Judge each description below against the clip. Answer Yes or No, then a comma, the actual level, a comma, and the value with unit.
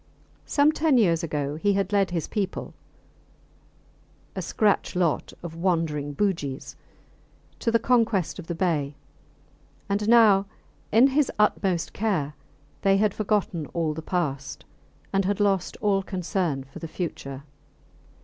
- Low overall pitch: No, medium, 185 Hz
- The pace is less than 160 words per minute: Yes, slow, 135 wpm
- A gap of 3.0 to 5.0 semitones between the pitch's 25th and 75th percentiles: Yes, average, 4.5 semitones